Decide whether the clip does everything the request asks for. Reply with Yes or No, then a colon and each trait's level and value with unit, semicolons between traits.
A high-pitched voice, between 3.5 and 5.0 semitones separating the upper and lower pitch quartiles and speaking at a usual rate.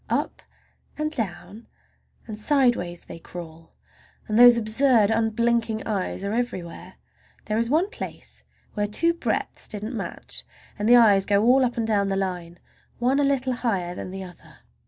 Yes: high, 220 Hz; average, 4.0 semitones; average, 160 wpm